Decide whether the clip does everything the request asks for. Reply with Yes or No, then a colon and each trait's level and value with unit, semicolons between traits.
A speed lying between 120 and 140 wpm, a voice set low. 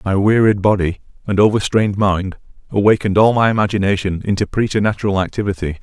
Yes: slow, 135 wpm; low, 100 Hz